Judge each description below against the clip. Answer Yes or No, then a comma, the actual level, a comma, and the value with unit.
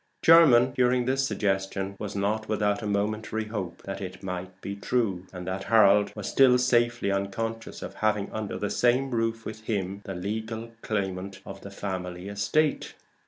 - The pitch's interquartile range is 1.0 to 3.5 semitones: Yes, average, 2.7 semitones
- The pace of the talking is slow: No, average, 165 wpm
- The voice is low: Yes, low, 105 Hz